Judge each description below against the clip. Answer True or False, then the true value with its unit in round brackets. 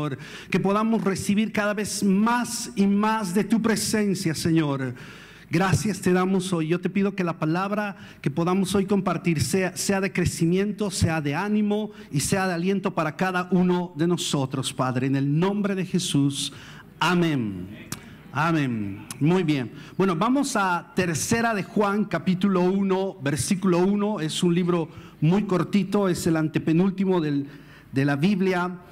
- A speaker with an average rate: True (155 wpm)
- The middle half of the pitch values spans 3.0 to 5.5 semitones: True (4.0 semitones)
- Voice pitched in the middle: True (180 Hz)